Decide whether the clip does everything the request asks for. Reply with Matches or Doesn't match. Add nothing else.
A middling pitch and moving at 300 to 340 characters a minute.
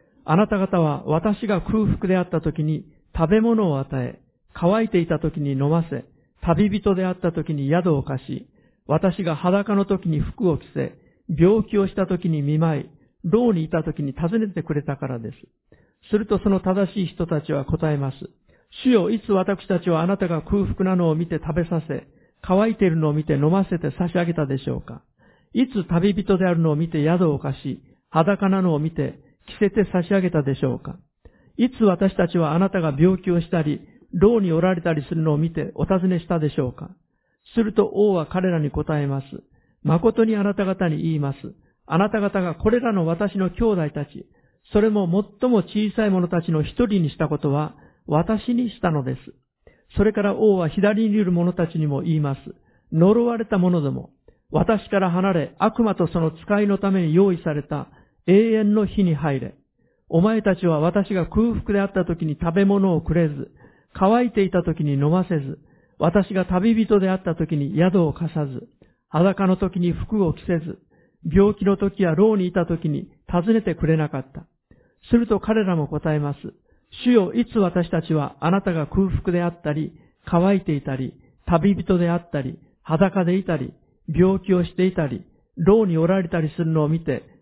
Matches